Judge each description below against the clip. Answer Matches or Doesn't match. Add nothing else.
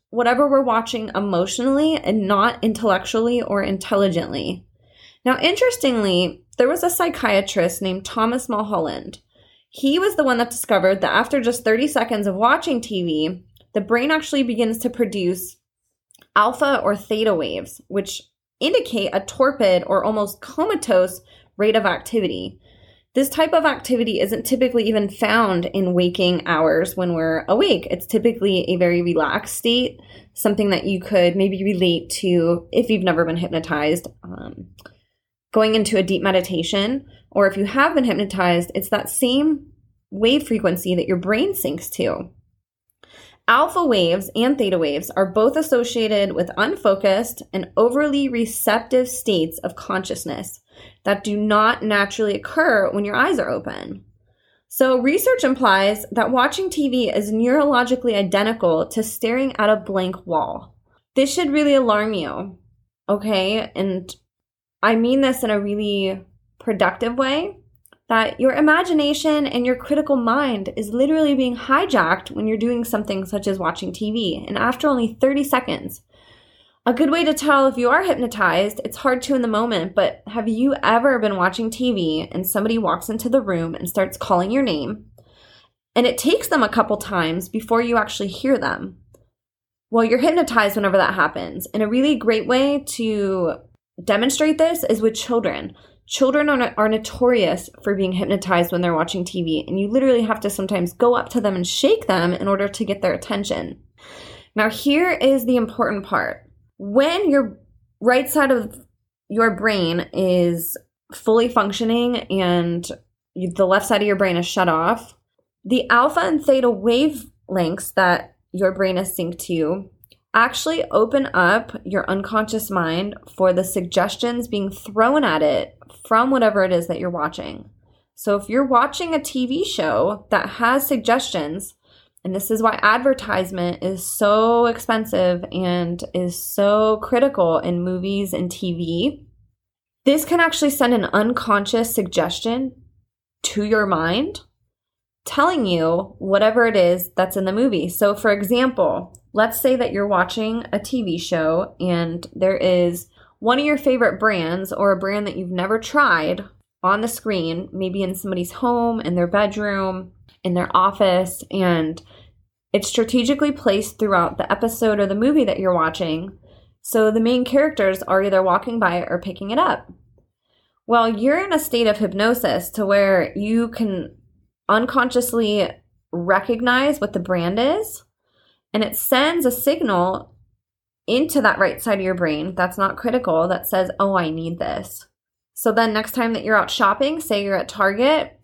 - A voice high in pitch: Matches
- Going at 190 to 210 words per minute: Doesn't match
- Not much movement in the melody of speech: Doesn't match